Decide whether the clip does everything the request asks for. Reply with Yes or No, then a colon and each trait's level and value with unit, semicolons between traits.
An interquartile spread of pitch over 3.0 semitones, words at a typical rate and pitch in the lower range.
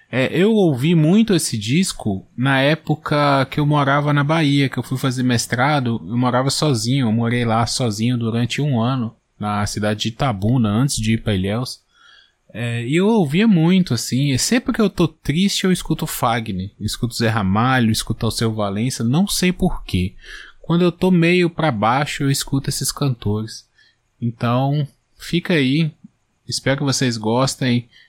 Yes: average, 5.1 semitones; average, 165 wpm; low, 130 Hz